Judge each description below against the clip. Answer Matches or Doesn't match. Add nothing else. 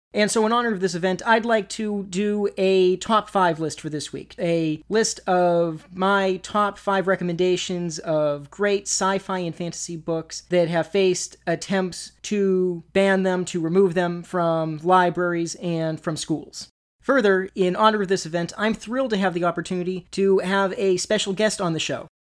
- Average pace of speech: Matches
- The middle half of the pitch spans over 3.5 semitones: Doesn't match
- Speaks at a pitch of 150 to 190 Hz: Matches